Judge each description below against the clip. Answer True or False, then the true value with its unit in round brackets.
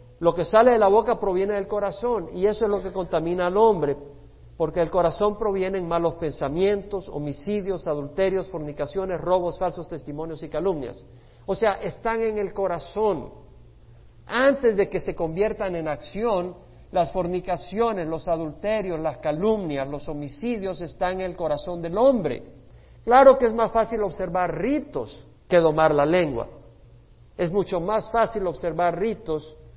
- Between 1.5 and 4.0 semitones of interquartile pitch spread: False (4.4 semitones)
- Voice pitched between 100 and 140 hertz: False (180 Hz)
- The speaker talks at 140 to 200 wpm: True (150 wpm)